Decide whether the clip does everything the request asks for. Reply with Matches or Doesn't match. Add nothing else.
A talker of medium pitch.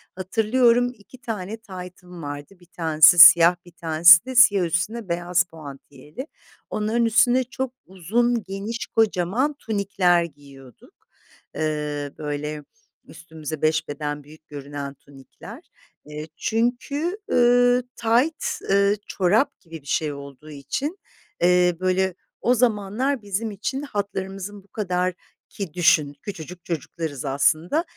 Matches